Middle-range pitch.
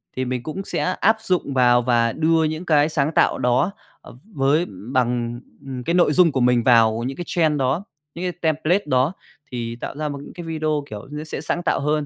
Yes: medium, 145 Hz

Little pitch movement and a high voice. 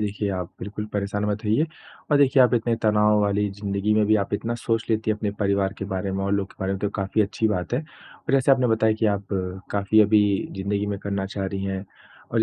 No: narrow, 1.8 semitones; low, 105 Hz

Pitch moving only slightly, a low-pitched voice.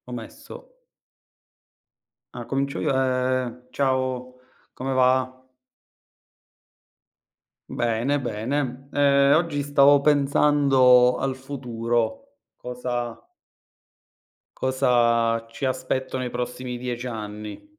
Yes: narrow, 2.2 semitones; low, 130 Hz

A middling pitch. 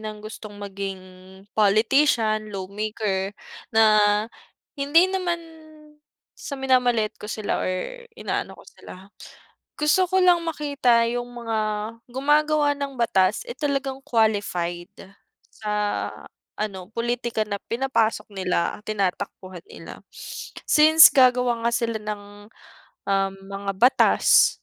No: high, 225 Hz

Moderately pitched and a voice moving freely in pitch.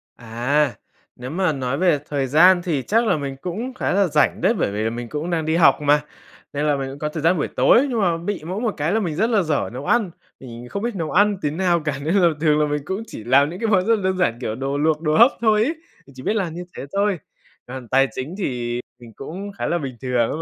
Yes: medium, 155 Hz; wide, 5.7 semitones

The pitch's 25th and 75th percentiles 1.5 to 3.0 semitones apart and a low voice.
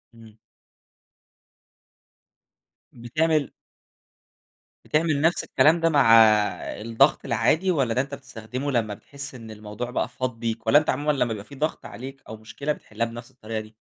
No: average, 4.2 semitones; low, 125 Hz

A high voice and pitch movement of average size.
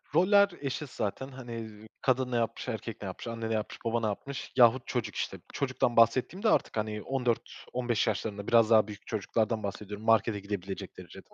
No: low, 115 Hz; average, 3.1 semitones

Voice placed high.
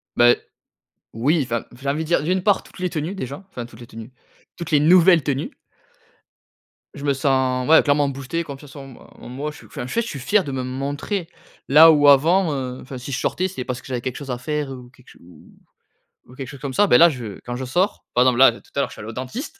No: medium, 140 Hz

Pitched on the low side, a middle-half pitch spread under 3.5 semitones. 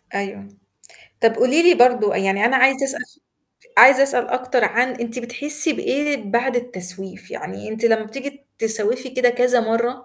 No: high, 245 Hz; average, 3.1 semitones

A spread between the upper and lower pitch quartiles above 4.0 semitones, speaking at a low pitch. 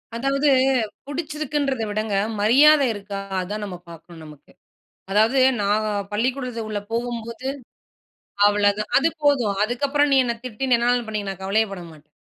No: average, 4.7 semitones; high, 225 Hz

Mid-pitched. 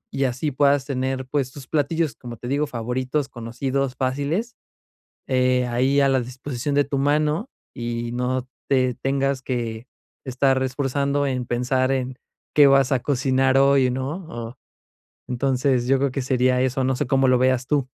No: low, 130 Hz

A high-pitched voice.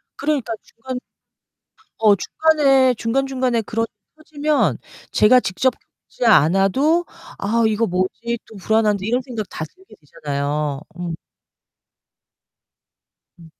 Yes: high, 225 Hz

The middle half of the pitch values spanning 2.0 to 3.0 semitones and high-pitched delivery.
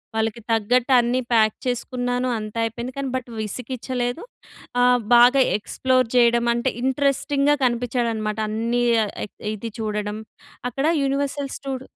Yes: narrow, 2.5 semitones; high, 245 Hz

